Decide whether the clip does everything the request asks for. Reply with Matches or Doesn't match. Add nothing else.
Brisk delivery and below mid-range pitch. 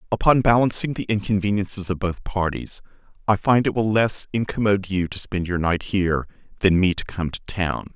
Doesn't match